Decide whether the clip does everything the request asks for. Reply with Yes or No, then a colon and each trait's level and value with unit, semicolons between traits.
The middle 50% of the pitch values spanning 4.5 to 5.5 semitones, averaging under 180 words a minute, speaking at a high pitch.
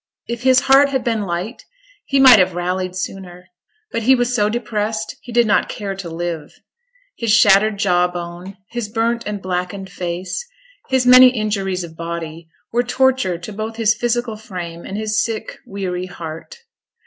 Yes: average, 4.8 semitones; average, 170 wpm; high, 205 Hz